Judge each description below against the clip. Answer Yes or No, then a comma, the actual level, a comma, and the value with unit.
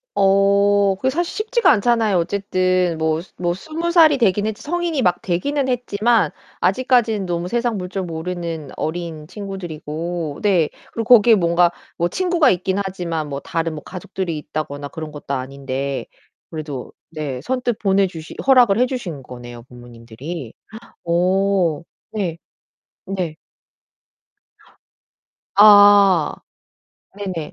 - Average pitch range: Yes, average, 5.0 semitones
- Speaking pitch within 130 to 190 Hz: Yes, medium, 185 Hz